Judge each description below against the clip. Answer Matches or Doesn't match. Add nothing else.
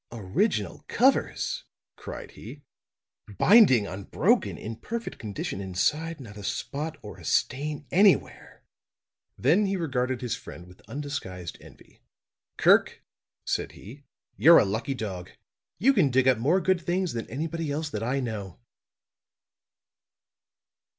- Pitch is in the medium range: Doesn't match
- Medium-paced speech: Doesn't match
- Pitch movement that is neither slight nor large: Doesn't match